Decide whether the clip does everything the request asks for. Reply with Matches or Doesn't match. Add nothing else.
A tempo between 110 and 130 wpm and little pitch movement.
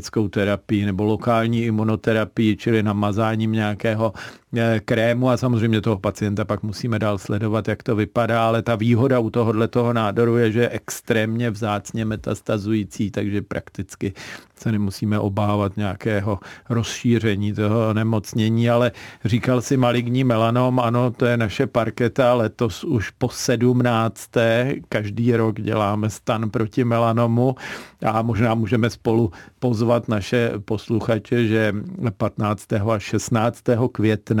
Matches